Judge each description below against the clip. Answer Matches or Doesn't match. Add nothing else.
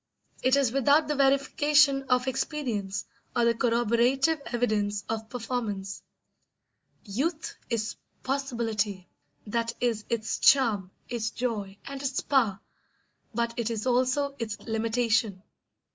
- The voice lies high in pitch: Matches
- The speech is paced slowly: Matches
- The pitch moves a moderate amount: Matches